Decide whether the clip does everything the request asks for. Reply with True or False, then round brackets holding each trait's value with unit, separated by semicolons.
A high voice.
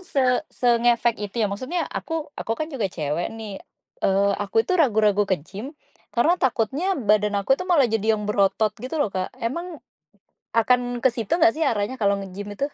True (230 Hz)